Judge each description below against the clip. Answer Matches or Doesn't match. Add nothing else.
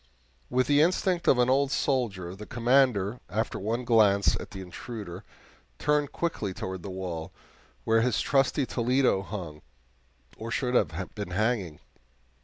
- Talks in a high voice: Doesn't match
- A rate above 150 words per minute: Doesn't match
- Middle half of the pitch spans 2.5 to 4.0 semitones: Doesn't match